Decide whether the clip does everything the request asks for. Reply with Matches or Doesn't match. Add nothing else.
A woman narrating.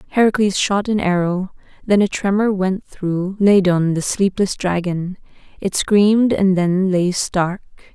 Matches